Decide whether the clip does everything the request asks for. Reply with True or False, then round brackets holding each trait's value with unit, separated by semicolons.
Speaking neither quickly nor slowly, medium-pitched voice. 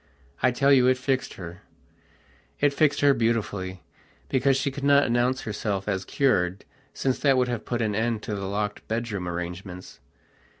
False (170 wpm; 115 Hz)